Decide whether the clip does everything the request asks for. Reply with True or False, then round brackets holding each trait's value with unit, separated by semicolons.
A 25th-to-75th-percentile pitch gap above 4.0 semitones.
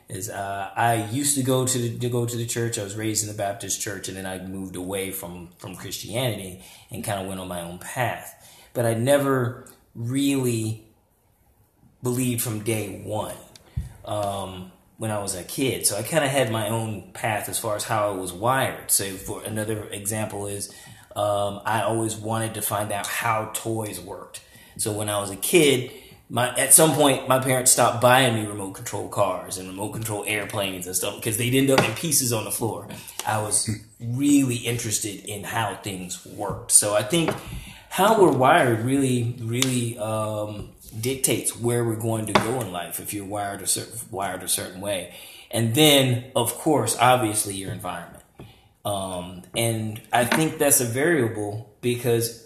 False (3.1 semitones)